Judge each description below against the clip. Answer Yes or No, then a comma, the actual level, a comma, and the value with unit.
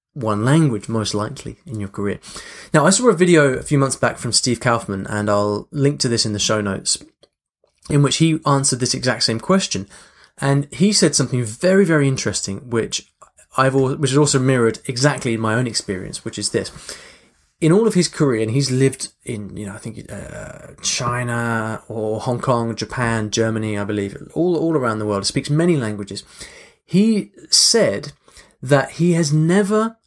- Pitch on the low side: Yes, low, 130 Hz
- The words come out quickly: No, average, 185 wpm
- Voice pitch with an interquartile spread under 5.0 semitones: No, average, 5.3 semitones